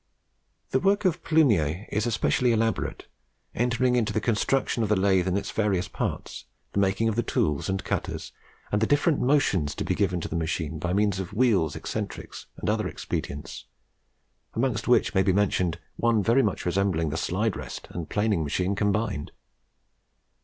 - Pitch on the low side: Yes, low, 105 Hz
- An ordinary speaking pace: Yes, average, 175 wpm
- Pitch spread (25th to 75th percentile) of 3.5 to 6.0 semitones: Yes, average, 4.4 semitones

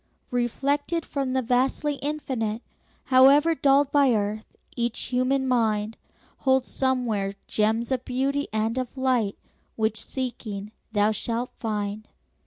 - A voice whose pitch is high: Yes, very high, 250 Hz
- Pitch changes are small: No, average, 3.6 semitones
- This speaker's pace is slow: Yes, slow, 120 wpm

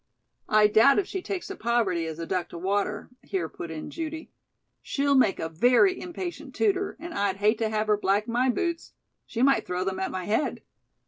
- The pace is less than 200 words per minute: No, fast, 205 wpm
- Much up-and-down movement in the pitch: Yes, wide, 8.0 semitones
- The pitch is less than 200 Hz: No, high, 215 Hz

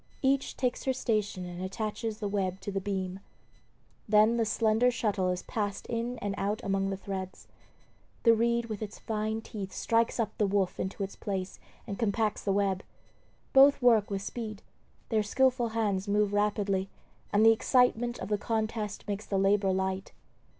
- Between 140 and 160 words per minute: No, average, 170 wpm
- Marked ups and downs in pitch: No, average, 2.7 semitones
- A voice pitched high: Yes, high, 210 Hz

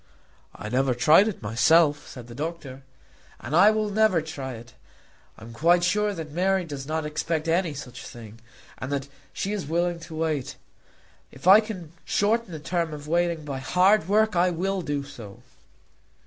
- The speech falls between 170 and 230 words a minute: Yes, average, 175 wpm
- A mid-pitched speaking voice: Yes, medium, 160 Hz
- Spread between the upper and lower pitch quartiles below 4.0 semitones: No, average, 4.8 semitones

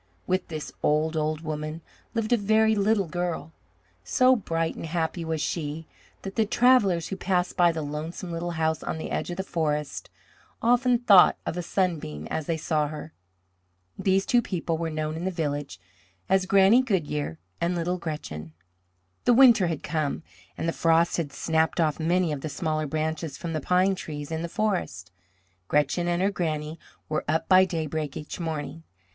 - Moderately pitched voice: Yes, medium, 165 Hz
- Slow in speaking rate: No, average, 180 wpm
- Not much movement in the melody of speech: No, average, 3.2 semitones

